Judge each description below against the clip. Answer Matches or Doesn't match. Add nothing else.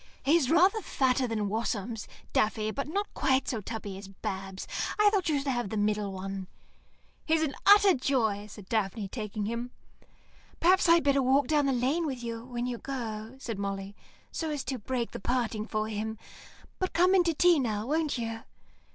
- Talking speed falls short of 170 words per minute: Doesn't match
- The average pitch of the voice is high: Matches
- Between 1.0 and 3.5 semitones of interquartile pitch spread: Doesn't match